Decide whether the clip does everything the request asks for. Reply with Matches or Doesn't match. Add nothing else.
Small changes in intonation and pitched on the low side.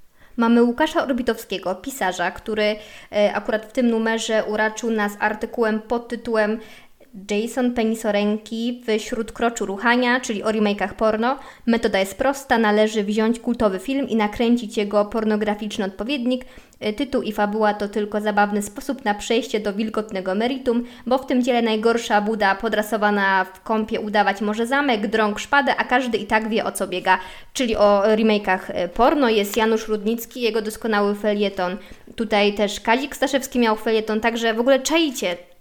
Doesn't match